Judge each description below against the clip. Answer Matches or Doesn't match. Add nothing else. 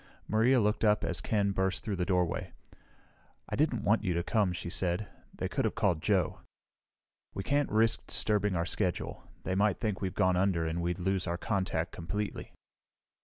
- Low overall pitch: Matches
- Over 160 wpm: Matches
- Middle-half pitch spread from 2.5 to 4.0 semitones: Matches